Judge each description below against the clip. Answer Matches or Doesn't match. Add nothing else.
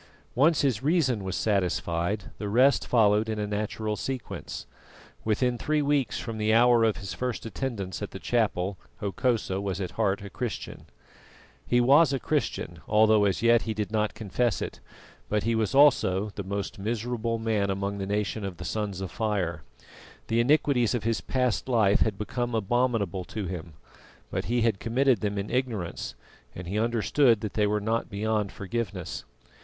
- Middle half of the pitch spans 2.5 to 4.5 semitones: Matches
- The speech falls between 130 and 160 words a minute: Doesn't match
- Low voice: Matches